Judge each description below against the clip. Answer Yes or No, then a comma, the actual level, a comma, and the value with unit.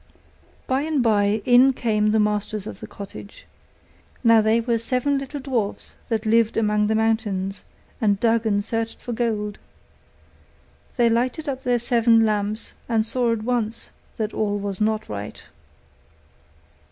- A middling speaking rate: Yes, average, 150 wpm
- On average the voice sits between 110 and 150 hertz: No, high, 225 Hz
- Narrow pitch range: Yes, narrow, 2.2 semitones